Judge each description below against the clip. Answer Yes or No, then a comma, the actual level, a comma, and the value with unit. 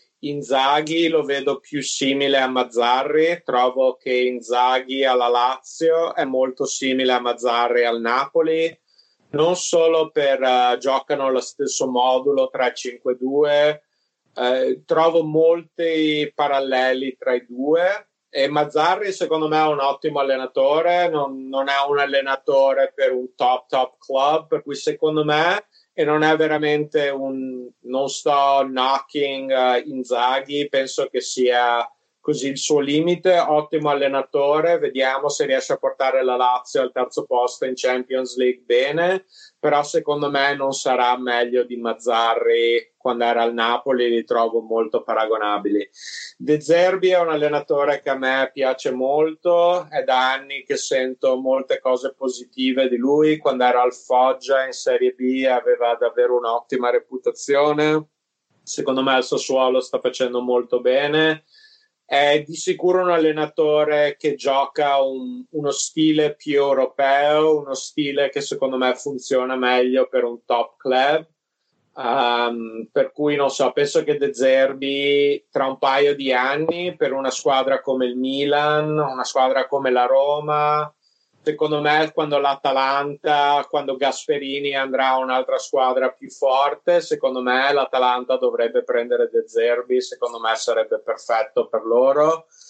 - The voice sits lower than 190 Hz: Yes, medium, 140 Hz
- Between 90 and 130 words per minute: No, average, 140 wpm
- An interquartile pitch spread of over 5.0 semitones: No, average, 3.1 semitones